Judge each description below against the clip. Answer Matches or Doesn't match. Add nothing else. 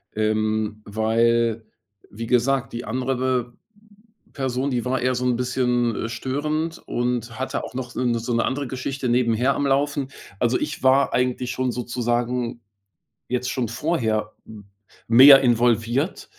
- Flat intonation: Matches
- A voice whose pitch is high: Doesn't match